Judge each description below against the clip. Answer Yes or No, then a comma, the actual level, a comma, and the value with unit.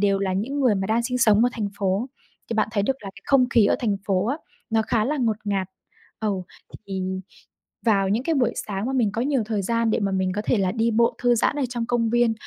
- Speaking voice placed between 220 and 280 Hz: Yes, high, 225 Hz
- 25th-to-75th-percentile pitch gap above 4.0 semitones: No, average, 3.2 semitones